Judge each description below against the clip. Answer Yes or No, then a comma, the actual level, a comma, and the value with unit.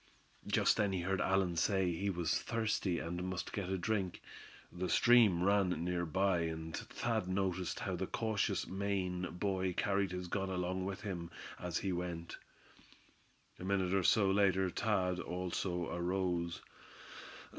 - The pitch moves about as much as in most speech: No, narrow, 1.9 semitones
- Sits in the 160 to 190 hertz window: No, very low, 95 Hz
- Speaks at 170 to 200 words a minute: No, average, 150 wpm